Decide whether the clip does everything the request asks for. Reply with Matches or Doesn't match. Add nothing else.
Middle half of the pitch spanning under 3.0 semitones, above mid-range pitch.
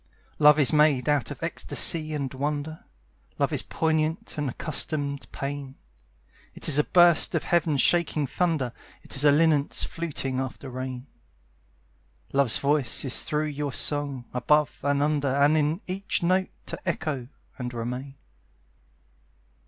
Doesn't match